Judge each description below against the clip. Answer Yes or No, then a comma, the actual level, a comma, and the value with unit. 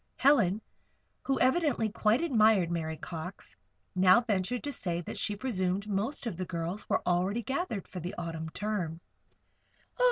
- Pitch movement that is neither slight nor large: Yes, average, 5.0 semitones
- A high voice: Yes, high, 200 Hz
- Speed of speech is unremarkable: Yes, average, 150 wpm